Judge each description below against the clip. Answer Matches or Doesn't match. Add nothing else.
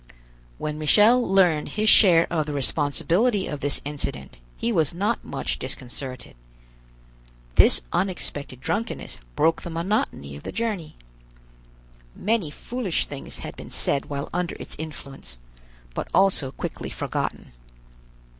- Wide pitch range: Matches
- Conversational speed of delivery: Doesn't match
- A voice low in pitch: Doesn't match